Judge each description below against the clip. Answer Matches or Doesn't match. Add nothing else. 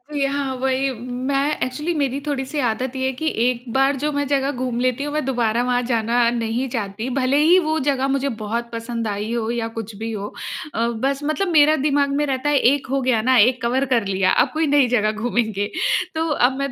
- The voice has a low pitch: Doesn't match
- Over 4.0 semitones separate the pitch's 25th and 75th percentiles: Doesn't match